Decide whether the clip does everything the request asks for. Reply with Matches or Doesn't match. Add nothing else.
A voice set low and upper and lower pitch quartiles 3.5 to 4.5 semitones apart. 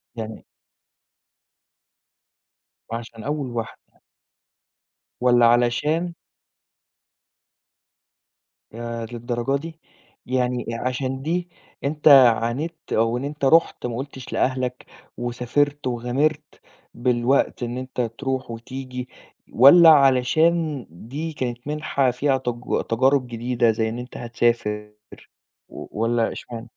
Doesn't match